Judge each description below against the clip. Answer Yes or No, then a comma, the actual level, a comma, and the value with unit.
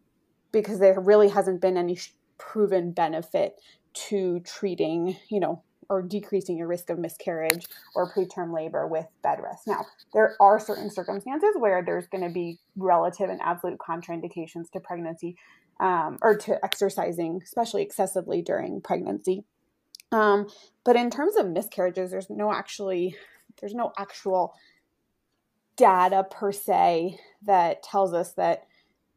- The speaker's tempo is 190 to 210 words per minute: No, average, 140 wpm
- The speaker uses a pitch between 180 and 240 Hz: Yes, high, 190 Hz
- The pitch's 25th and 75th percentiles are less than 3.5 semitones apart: Yes, average, 2.7 semitones